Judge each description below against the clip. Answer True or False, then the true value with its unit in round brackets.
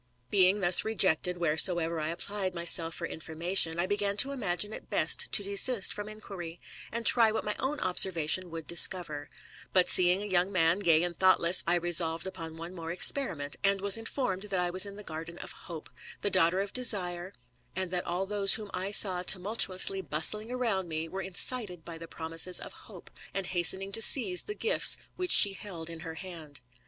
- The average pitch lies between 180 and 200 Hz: True (185 Hz)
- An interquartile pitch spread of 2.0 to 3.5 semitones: True (3.2 semitones)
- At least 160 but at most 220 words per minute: True (195 wpm)